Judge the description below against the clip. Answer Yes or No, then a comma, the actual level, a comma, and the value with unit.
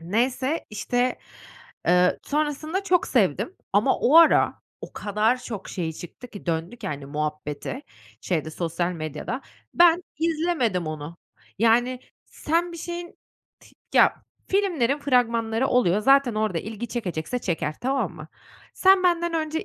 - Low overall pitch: No, high, 240 Hz